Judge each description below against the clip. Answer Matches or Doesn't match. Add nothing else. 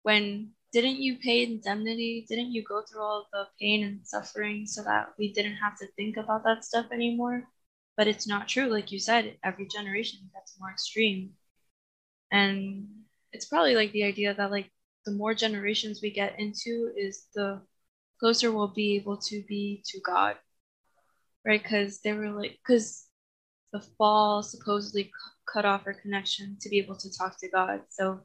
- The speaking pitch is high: Matches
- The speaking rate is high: Doesn't match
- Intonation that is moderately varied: Doesn't match